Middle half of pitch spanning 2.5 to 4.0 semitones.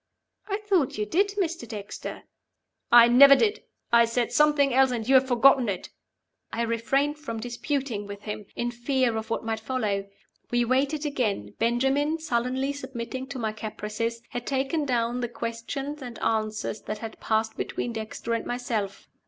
Yes: average, 3.5 semitones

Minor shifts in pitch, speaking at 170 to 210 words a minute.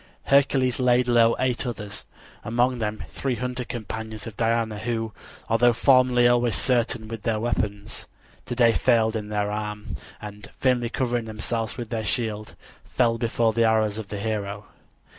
No: narrow, 2.2 semitones; average, 155 wpm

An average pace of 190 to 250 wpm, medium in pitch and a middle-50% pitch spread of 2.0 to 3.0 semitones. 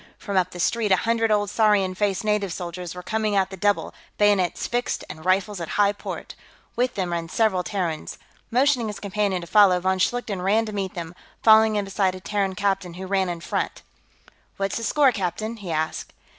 No: average, 200 wpm; high, 195 Hz; average, 2.7 semitones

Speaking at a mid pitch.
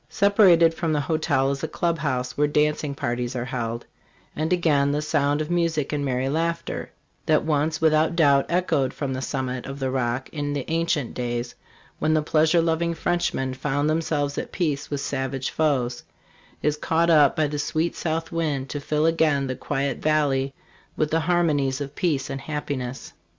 Yes: medium, 150 Hz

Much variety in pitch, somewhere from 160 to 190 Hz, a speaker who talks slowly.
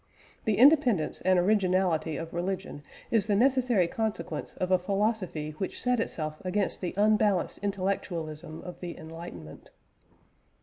No: average, 3.8 semitones; medium, 185 Hz; slow, 130 wpm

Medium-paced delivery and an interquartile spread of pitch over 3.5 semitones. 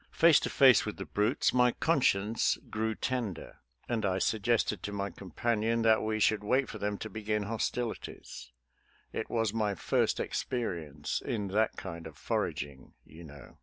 No: average, 170 wpm; average, 3.0 semitones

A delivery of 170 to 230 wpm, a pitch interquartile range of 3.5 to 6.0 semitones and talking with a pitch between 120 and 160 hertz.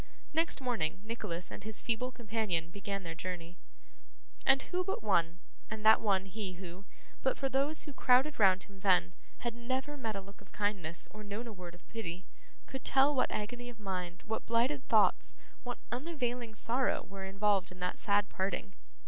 No: average, 180 wpm; average, 4.6 semitones; high, 210 Hz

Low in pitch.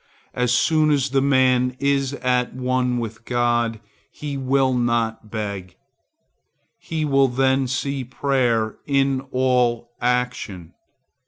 Yes: low, 125 Hz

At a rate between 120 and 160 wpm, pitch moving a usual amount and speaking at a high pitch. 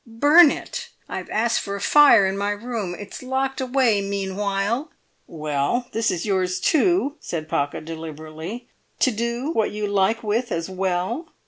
Yes: average, 155 wpm; average, 4.9 semitones; high, 210 Hz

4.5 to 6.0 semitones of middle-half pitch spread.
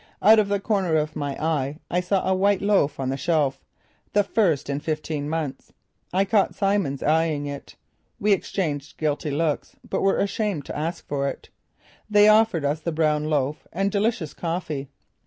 Yes: average, 5.2 semitones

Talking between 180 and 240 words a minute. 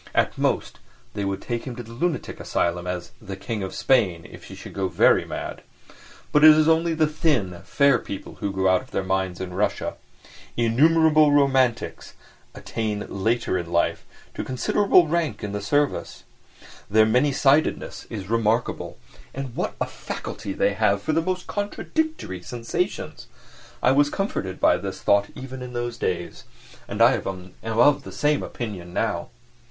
No: average, 170 wpm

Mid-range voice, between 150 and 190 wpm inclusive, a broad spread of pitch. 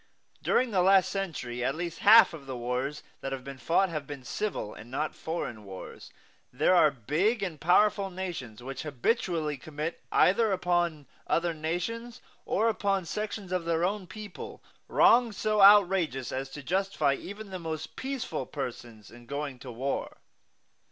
Yes: medium, 165 Hz; average, 160 wpm; wide, 6.4 semitones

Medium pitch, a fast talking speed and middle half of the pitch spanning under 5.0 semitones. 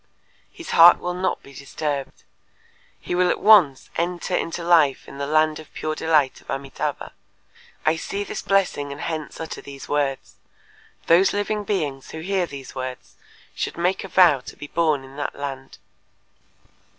No: medium, 155 Hz; average, 165 wpm; average, 4.1 semitones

